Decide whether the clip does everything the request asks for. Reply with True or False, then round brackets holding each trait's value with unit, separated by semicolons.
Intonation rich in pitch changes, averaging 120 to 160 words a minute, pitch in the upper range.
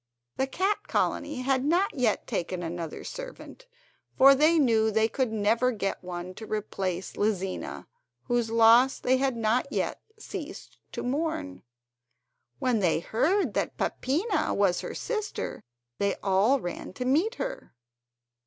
True (6.5 semitones; 140 wpm; 245 Hz)